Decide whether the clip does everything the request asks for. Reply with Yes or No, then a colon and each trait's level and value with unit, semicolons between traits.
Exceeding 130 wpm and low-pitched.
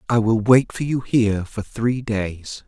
Yes: average, 200 wpm; low, 115 Hz